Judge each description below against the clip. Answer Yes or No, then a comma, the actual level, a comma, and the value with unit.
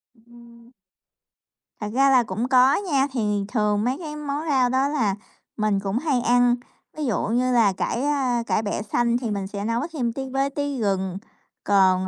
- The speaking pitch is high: Yes, high, 240 Hz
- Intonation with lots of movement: No, average, 4.3 semitones